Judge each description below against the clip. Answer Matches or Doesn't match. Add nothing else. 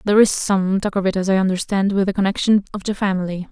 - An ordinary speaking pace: Doesn't match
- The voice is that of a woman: Matches